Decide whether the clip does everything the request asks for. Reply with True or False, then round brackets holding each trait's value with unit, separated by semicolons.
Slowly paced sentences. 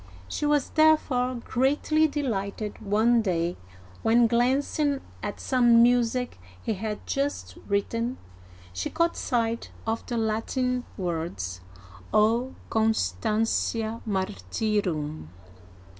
True (100 wpm)